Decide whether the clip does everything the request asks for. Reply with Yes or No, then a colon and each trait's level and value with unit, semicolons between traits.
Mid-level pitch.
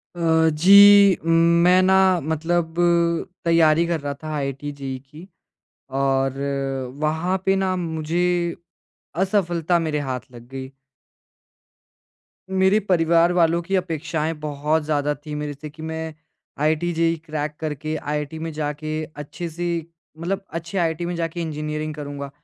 Yes: medium, 160 Hz